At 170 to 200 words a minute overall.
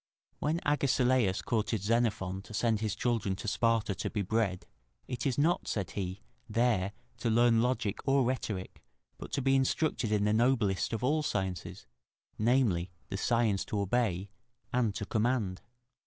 No: average, 155 wpm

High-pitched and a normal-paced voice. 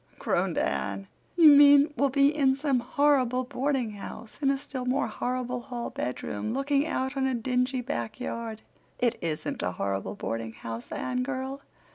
Yes: very high, 255 Hz; average, 155 wpm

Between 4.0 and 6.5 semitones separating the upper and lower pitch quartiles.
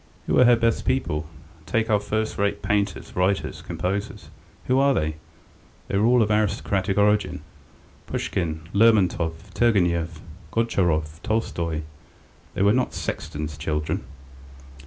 Yes: average, 4.9 semitones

